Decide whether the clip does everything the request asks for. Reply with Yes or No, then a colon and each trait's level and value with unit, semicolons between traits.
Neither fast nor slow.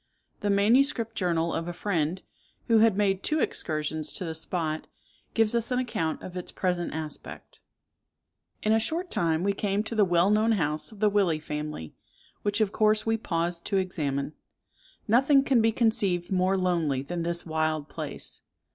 Yes: average, 175 wpm